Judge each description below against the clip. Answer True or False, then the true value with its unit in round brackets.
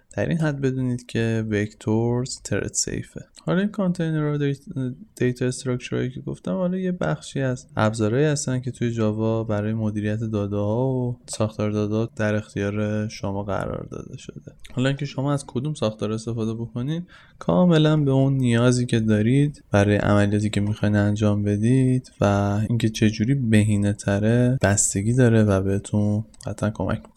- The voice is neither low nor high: False (115 Hz)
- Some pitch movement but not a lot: True (3.7 semitones)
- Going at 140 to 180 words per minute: True (150 wpm)